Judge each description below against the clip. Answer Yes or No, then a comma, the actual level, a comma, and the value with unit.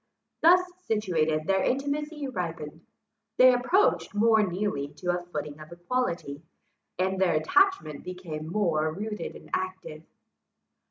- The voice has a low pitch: No, medium, 185 Hz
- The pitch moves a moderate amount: No, wide, 6.4 semitones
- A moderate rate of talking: No, slow, 120 wpm